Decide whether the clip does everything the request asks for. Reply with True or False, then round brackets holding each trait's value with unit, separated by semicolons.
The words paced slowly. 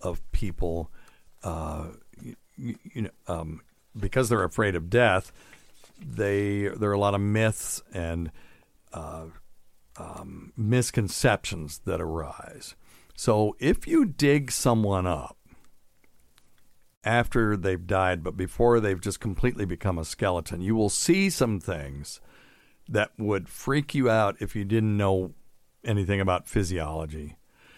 True (125 wpm)